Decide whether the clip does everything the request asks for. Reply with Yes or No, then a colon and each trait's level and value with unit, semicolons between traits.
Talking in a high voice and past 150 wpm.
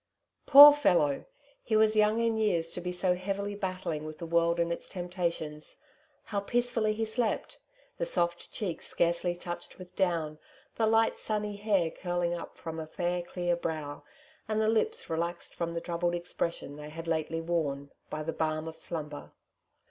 No: medium, 175 Hz; average, 170 wpm